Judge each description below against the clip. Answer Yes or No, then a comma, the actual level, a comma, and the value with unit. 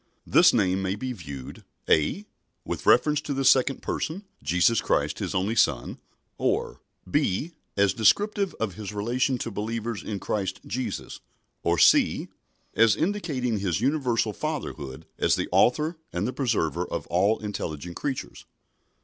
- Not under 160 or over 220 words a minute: No, average, 145 wpm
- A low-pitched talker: Yes, low, 110 Hz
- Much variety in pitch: Yes, wide, 6.0 semitones